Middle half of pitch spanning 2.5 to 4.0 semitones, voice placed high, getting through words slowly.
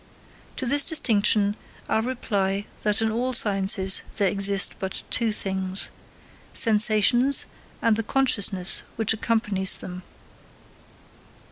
Yes: average, 2.9 semitones; high, 210 Hz; slow, 110 wpm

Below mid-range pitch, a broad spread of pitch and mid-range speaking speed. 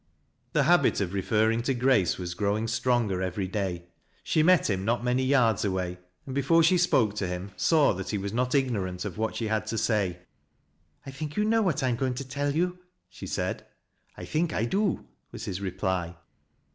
No: low, 115 Hz; wide, 6.4 semitones; fast, 210 wpm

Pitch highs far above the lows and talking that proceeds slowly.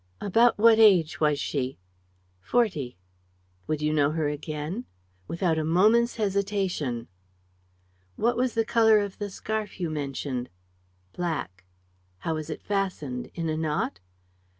Yes: wide, 5.9 semitones; slow, 130 wpm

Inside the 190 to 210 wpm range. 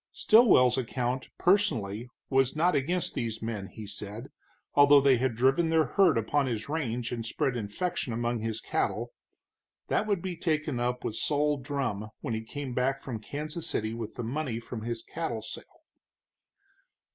No: average, 165 wpm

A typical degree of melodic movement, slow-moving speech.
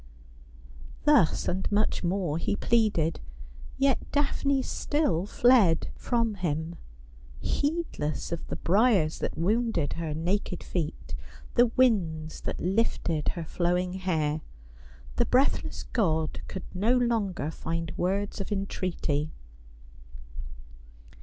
No: wide, 5.9 semitones; slow, 105 wpm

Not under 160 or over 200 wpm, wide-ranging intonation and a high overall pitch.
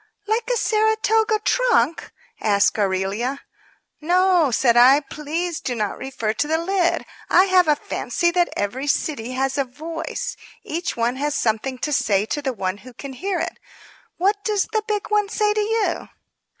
Yes: average, 170 wpm; wide, 8.1 semitones; very high, 305 Hz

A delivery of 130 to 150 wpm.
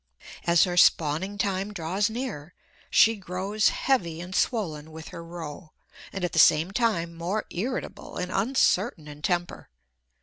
Yes: average, 145 wpm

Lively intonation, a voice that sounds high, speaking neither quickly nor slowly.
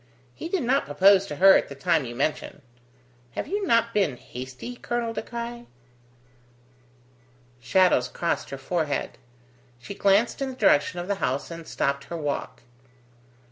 No: wide, 8.5 semitones; medium, 180 Hz; average, 155 wpm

